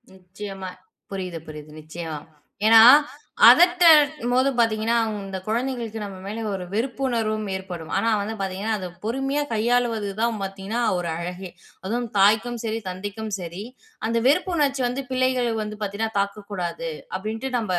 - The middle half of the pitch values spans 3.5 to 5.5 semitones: Yes, average, 4.0 semitones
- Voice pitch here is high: Yes, high, 220 Hz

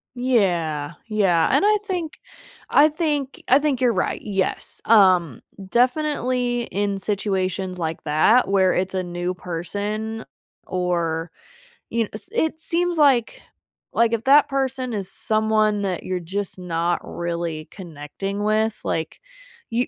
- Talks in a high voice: Yes, high, 205 Hz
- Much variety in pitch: Yes, wide, 5.7 semitones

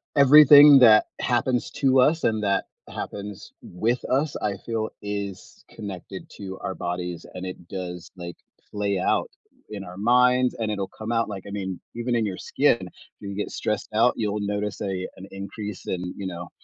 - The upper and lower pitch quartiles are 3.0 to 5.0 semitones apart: Yes, average, 3.8 semitones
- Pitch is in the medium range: No, low, 105 Hz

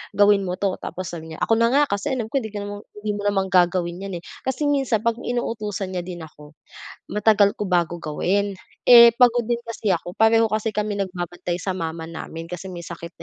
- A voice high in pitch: Yes, high, 200 Hz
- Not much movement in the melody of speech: No, average, 4.1 semitones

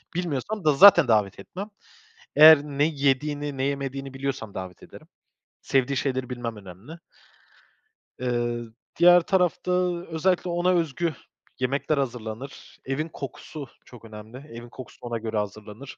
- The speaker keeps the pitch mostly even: No, average, 4.7 semitones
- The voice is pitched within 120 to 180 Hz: Yes, low, 135 Hz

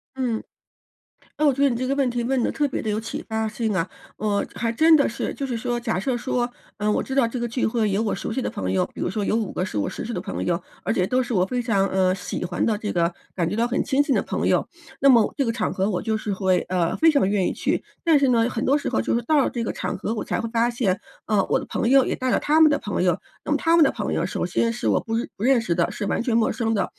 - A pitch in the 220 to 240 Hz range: Yes, high, 230 Hz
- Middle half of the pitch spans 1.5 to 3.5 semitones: No, average, 4.0 semitones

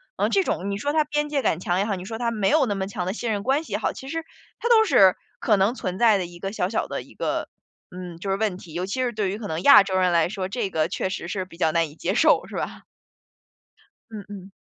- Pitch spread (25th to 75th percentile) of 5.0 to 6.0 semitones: No, average, 4.5 semitones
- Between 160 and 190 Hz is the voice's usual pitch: No, high, 200 Hz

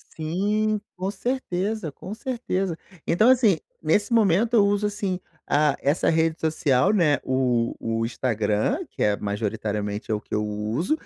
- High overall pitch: No, medium, 165 Hz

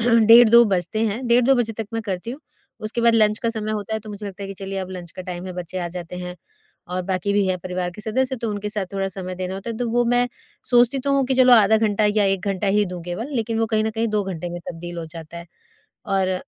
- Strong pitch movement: No, average, 3.7 semitones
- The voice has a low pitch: No, high, 205 Hz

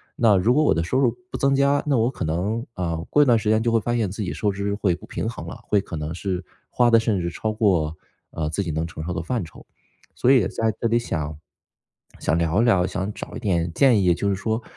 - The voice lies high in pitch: No, low, 100 Hz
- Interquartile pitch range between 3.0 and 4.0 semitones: No, average, 5.1 semitones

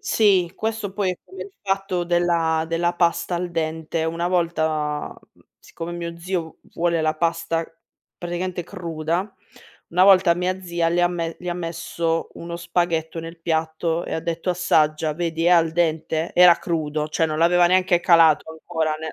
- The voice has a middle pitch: Yes, medium, 170 Hz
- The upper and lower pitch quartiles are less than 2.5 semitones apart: Yes, narrow, 1.5 semitones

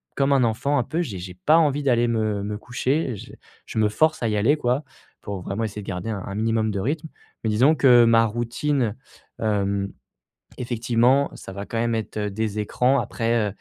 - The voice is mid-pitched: No, low, 115 Hz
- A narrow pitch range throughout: No, average, 3.7 semitones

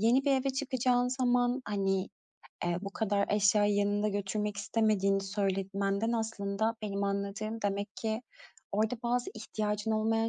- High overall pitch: Yes, high, 210 Hz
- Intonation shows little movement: Yes, narrow, 2.3 semitones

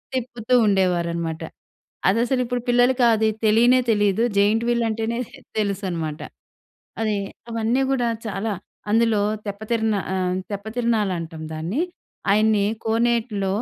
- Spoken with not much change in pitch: No, average, 3.1 semitones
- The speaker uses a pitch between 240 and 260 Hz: No, high, 220 Hz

